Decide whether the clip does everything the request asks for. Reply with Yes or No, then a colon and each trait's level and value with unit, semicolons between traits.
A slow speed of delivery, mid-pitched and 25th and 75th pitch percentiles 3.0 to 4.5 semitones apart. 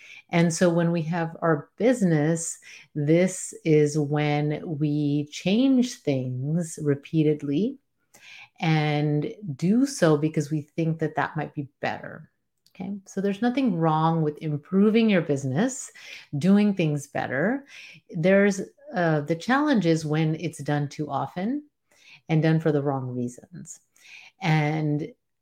Yes: slow, 125 wpm; medium, 160 Hz; average, 4.2 semitones